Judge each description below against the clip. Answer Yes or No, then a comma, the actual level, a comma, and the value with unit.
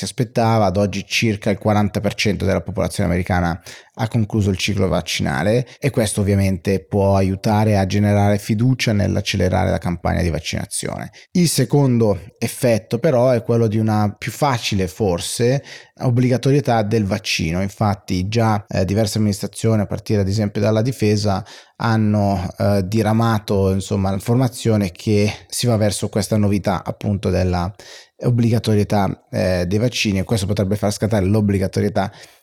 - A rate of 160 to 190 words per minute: No, average, 140 wpm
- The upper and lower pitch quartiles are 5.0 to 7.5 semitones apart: No, average, 2.7 semitones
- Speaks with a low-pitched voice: Yes, low, 105 Hz